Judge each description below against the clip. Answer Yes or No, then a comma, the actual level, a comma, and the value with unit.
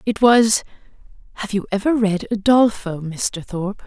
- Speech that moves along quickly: No, average, 140 wpm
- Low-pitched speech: No, high, 205 Hz